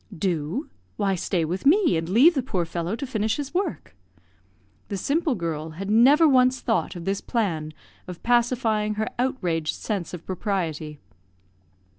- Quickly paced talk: No, average, 155 wpm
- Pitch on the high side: Yes, high, 210 Hz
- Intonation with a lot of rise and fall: Yes, wide, 6.9 semitones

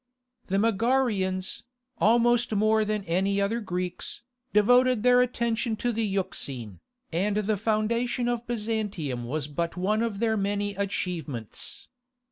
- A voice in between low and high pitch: No, high, 210 Hz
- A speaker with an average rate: No, slow, 125 wpm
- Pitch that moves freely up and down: No, average, 3.7 semitones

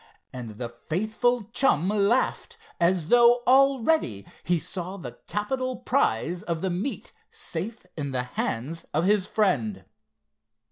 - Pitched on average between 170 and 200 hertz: Yes, medium, 185 Hz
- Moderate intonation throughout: No, wide, 8.0 semitones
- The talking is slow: Yes, slow, 130 wpm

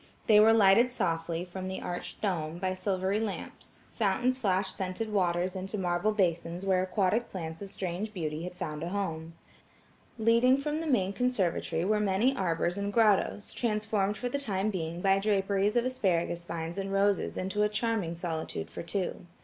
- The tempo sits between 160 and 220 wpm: Yes, average, 175 wpm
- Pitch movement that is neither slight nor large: Yes, average, 3.4 semitones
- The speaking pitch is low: No, high, 195 Hz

